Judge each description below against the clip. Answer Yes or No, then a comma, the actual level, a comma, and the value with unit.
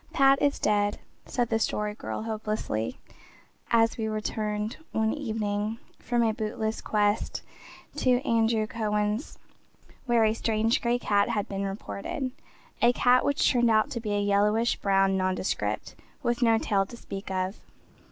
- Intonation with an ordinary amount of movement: No, narrow, 2.1 semitones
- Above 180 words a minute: No, average, 150 wpm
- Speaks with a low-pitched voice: No, high, 220 Hz